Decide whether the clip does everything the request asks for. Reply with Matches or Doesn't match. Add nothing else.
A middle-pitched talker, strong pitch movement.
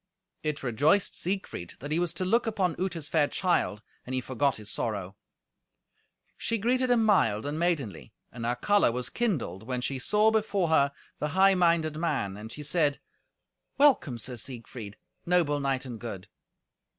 Matches